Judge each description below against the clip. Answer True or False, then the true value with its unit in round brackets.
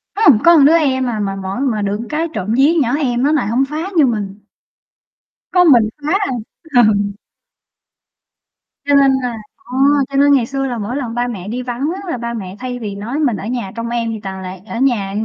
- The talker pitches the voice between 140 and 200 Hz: False (245 Hz)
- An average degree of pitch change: True (4.6 semitones)